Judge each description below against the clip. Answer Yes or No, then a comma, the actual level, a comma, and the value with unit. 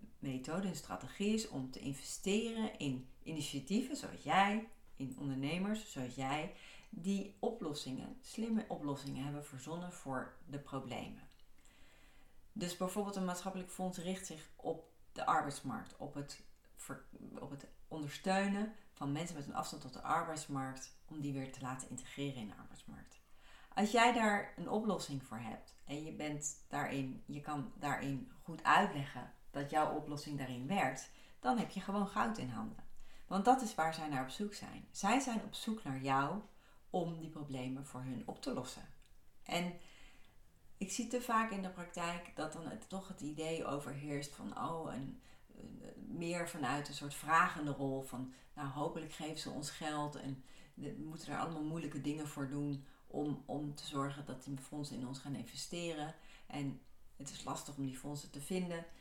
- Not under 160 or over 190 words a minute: Yes, average, 170 wpm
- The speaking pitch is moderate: Yes, medium, 150 Hz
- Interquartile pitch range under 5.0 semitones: No, average, 5.3 semitones